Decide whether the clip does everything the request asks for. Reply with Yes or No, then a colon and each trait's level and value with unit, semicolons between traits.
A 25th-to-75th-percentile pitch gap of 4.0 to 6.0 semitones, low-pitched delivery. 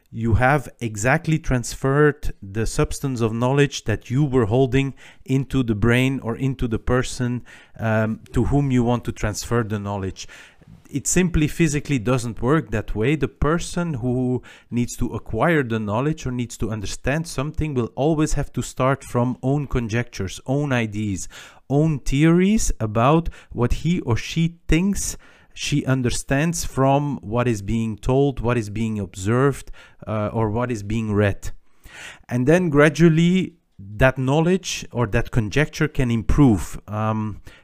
Yes: average, 4.3 semitones; low, 125 Hz